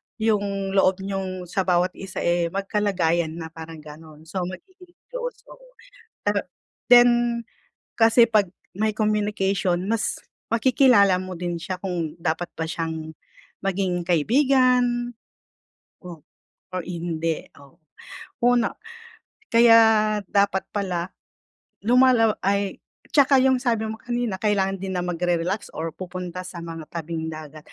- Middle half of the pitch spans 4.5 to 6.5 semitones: Yes, average, 4.8 semitones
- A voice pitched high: Yes, high, 195 Hz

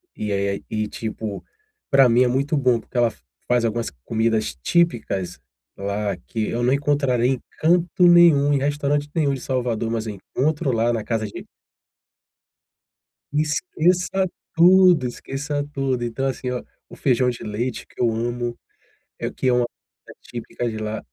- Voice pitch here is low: Yes, low, 125 Hz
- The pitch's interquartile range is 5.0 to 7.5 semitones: No, average, 4.2 semitones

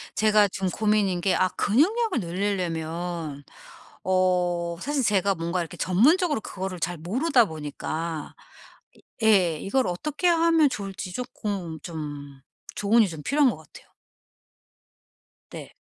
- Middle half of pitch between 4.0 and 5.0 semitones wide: No, wide, 5.4 semitones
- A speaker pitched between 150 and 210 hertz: Yes, medium, 185 Hz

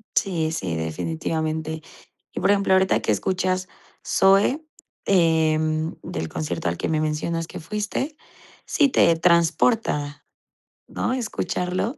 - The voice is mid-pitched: Yes, medium, 165 Hz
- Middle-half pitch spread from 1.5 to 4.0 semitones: Yes, average, 3.6 semitones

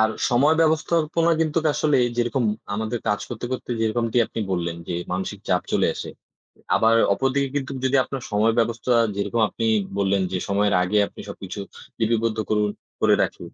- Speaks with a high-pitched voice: No, low, 115 Hz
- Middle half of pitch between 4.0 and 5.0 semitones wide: Yes, average, 4.5 semitones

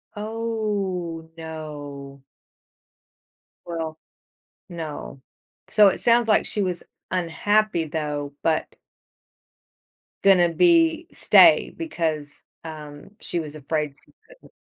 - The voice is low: No, medium, 165 Hz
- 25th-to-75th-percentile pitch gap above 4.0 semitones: Yes, wide, 5.5 semitones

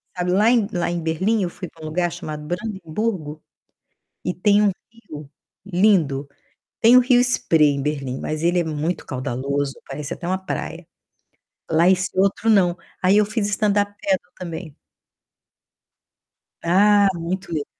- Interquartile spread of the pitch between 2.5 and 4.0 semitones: No, average, 4.7 semitones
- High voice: No, medium, 175 Hz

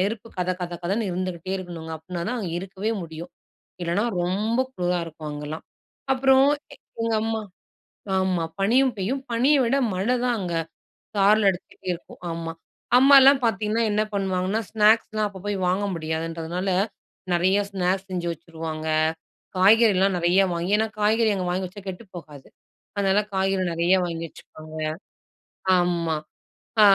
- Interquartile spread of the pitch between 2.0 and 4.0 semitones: Yes, average, 3.7 semitones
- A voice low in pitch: No, high, 190 Hz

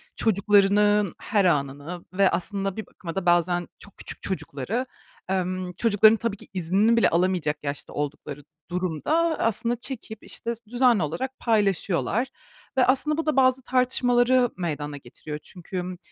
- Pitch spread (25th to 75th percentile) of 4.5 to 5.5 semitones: Yes, average, 5.2 semitones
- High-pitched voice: Yes, high, 195 Hz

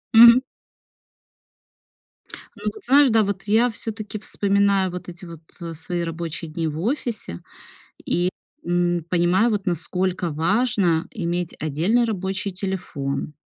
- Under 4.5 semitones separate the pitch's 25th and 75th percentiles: Yes, average, 4.1 semitones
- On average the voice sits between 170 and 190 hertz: Yes, medium, 185 Hz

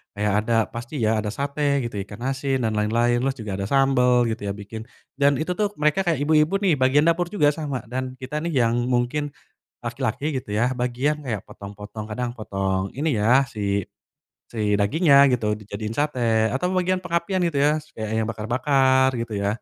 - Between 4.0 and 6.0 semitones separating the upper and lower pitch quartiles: Yes, average, 5.2 semitones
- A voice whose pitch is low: Yes, low, 125 Hz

